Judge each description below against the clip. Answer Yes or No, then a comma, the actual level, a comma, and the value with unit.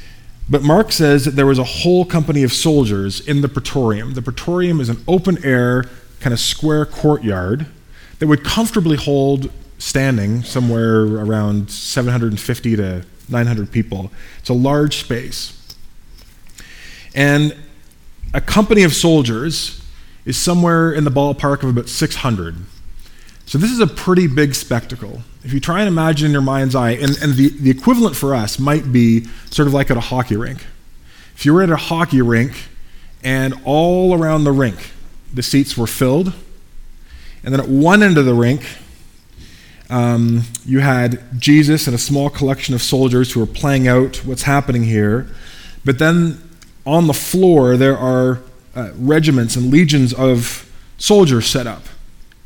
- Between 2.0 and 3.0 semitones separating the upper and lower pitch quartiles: No, average, 4.2 semitones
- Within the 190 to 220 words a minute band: No, average, 160 wpm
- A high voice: No, low, 130 Hz